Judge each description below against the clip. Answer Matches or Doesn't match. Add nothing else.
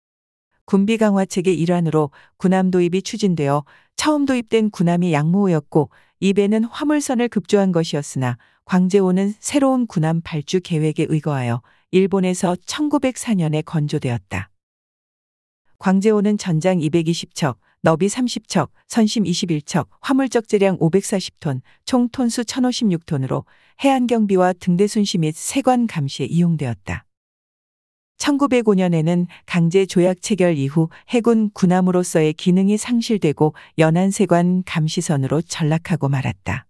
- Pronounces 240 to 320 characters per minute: Matches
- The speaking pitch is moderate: Matches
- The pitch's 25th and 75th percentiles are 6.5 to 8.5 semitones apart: Doesn't match